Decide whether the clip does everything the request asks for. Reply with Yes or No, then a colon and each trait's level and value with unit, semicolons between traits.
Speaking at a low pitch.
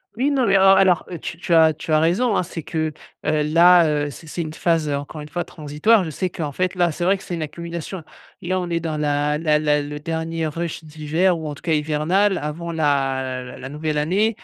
No: medium, 160 Hz